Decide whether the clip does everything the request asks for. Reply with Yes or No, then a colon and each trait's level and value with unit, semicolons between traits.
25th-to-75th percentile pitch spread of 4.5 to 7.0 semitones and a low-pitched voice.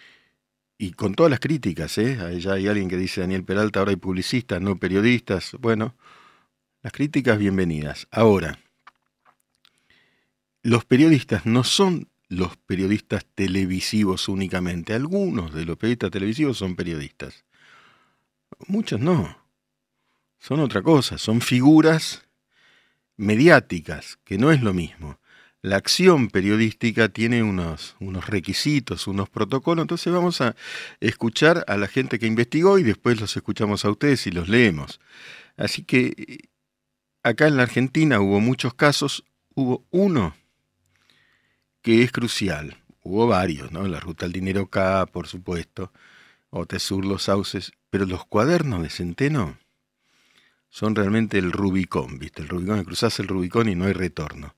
Yes: average, 5.0 semitones; low, 105 Hz